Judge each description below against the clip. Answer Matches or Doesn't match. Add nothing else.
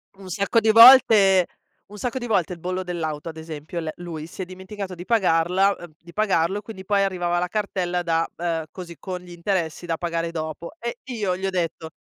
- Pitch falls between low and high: Matches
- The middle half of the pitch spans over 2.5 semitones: Matches